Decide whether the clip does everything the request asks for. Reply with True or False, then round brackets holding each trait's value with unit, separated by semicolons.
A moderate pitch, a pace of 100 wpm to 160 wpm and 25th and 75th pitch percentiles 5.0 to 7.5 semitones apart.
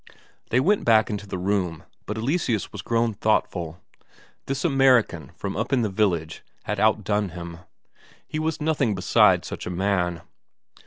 False (105 Hz; 155 wpm; 5.5 semitones)